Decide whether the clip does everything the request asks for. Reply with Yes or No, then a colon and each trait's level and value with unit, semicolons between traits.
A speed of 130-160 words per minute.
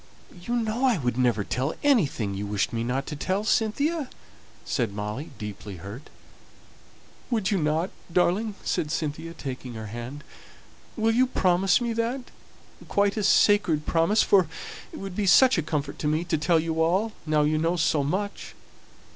No: average, 170 wpm